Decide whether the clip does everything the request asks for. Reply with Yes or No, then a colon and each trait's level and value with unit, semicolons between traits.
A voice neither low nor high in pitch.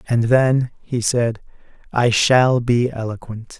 No: low, 120 Hz